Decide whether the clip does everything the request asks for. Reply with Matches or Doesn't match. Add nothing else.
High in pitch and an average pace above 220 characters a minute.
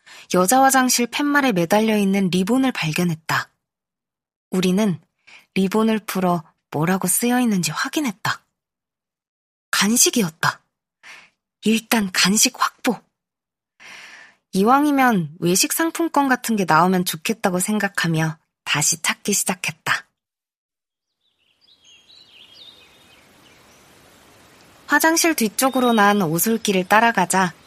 Doesn't match